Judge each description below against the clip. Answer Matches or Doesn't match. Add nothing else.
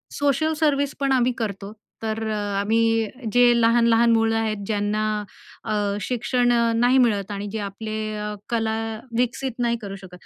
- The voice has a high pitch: Matches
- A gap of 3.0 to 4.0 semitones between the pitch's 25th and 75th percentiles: Doesn't match